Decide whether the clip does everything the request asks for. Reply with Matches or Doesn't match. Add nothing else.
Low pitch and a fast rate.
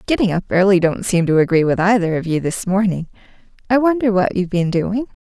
Doesn't match